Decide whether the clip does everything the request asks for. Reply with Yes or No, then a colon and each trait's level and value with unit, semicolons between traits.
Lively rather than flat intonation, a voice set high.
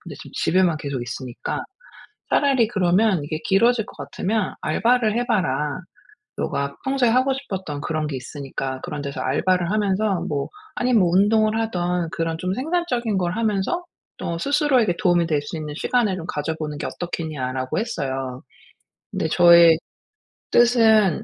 No: wide, 6.9 semitones; medium, 180 Hz